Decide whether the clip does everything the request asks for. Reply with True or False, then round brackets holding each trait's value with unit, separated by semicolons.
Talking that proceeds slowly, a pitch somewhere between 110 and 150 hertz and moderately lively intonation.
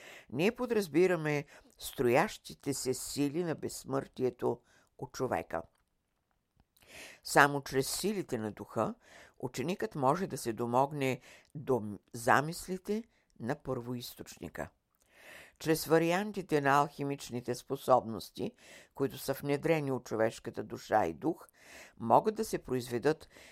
True (100 wpm; 140 Hz; 4.4 semitones)